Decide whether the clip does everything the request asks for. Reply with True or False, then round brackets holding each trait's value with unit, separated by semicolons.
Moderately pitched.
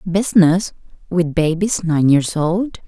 True (175 Hz)